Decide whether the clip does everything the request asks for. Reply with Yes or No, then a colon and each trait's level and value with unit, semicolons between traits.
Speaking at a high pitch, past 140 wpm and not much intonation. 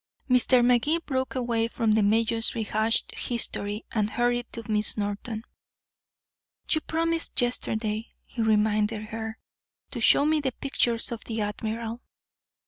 No: high, 230 Hz; slow, 135 wpm; narrow, 2.1 semitones